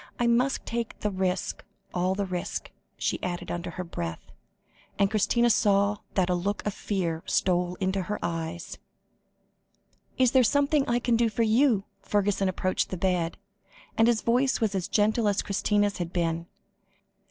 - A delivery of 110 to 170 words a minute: Yes, average, 165 wpm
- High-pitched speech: Yes, high, 200 Hz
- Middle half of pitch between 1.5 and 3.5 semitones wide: No, average, 4.2 semitones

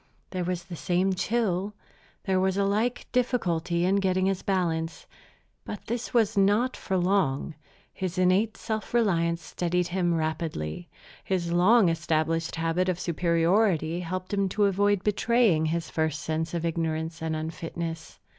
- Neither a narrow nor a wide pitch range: Yes, average, 3.2 semitones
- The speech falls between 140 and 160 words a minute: Yes, average, 145 wpm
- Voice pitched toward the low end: No, medium, 180 Hz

